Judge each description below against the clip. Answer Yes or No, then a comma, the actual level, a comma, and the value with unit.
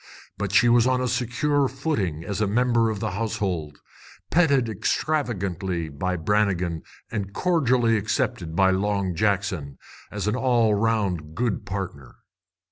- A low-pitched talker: Yes, low, 105 Hz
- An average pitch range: Yes, average, 4.6 semitones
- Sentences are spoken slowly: Yes, slow, 130 wpm